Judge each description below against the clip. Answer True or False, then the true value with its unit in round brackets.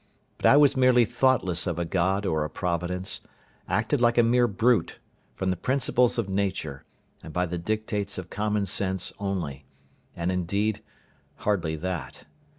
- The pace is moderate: True (155 wpm)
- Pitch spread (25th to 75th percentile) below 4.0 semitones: False (4.4 semitones)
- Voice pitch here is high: False (95 Hz)